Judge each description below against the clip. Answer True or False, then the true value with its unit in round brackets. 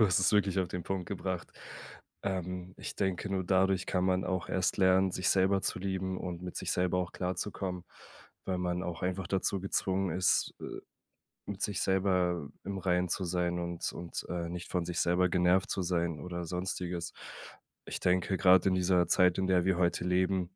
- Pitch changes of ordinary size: False (1.2 semitones)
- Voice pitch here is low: True (90 Hz)